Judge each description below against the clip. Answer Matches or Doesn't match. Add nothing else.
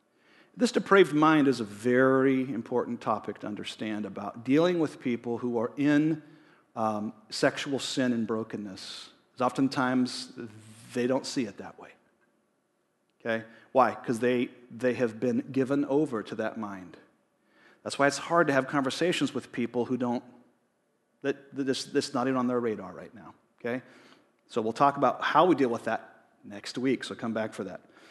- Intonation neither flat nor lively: Matches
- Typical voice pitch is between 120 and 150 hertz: Matches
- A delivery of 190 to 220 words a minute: Doesn't match